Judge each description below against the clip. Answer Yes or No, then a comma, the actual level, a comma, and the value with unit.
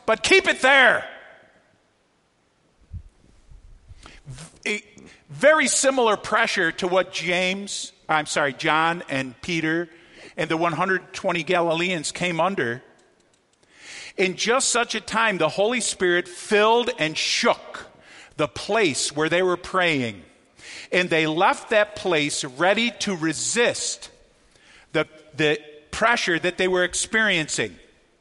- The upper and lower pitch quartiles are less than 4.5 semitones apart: No, average, 4.9 semitones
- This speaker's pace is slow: Yes, slow, 115 wpm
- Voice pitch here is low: No, medium, 180 Hz